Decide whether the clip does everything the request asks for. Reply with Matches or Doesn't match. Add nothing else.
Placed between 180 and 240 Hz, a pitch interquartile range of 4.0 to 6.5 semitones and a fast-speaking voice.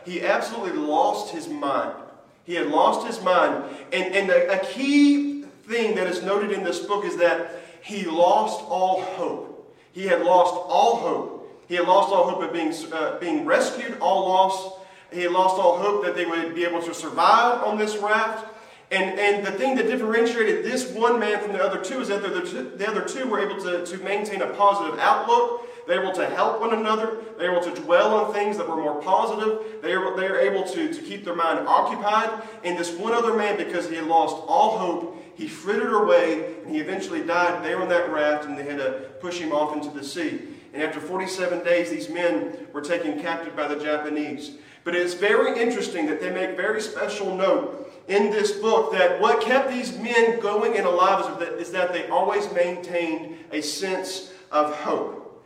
Matches